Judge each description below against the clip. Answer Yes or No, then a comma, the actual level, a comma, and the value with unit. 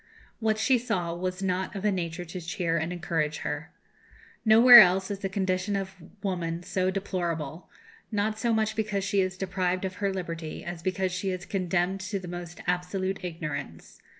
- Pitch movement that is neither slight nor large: No, narrow, 2.1 semitones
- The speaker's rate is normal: Yes, average, 180 wpm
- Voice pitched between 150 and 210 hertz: Yes, medium, 185 Hz